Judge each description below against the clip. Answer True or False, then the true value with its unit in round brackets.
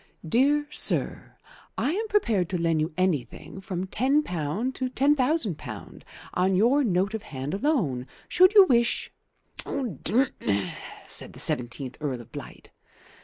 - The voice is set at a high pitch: True (195 Hz)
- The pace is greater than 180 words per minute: False (140 wpm)